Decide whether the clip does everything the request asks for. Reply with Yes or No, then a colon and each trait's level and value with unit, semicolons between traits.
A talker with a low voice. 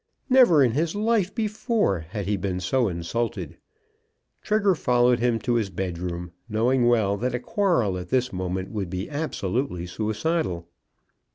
Yes: low, 115 Hz